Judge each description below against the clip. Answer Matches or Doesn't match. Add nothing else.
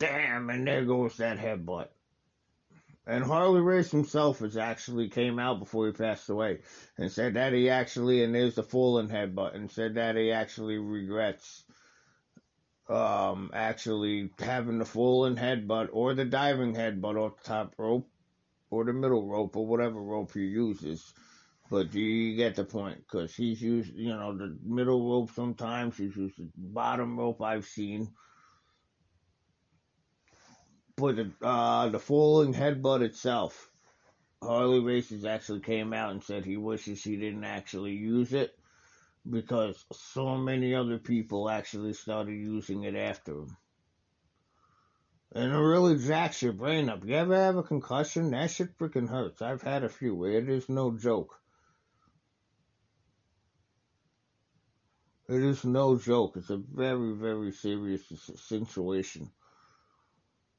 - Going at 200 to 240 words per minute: Doesn't match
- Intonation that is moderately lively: Matches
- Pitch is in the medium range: Doesn't match